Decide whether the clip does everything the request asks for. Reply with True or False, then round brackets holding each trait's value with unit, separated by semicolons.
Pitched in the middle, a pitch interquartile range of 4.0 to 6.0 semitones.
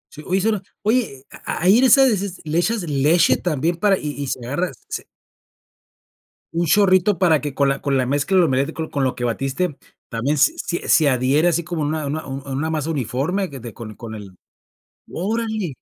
True (155 Hz; 5.1 semitones)